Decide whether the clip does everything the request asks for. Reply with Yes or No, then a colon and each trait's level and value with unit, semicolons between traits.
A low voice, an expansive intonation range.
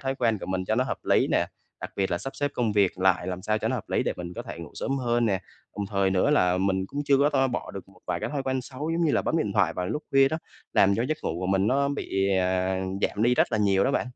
Yes: low, 105 Hz; wide, 6.1 semitones